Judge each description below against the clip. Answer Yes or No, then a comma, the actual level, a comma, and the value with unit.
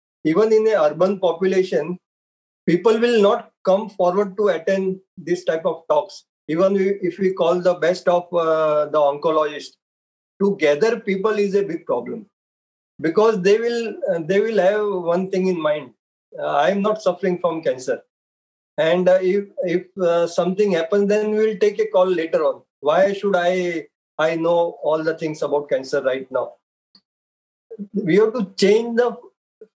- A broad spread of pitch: No, average, 3.8 semitones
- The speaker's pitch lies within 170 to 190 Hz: Yes, medium, 185 Hz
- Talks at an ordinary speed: Yes, average, 165 wpm